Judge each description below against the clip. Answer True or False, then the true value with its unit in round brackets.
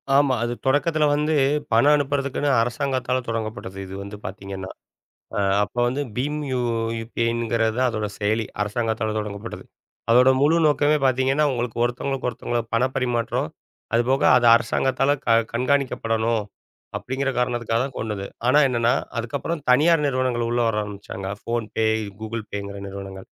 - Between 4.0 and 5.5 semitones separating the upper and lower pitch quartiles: False (3.4 semitones)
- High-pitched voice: False (120 Hz)